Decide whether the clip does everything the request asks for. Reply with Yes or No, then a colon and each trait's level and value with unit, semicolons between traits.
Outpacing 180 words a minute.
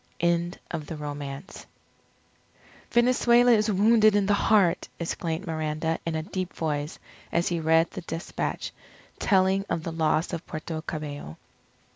No: average, 140 wpm